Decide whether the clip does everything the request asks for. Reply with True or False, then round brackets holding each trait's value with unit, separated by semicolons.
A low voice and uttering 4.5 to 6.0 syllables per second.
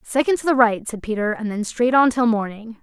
False (230 Hz; 5.5 syllables/s)